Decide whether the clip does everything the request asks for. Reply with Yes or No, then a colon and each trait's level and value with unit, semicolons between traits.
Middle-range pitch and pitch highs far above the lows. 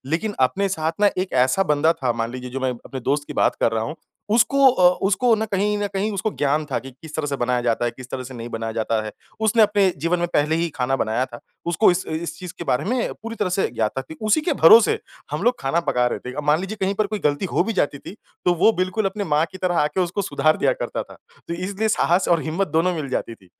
Yes: medium, 165 Hz; wide, 6.9 semitones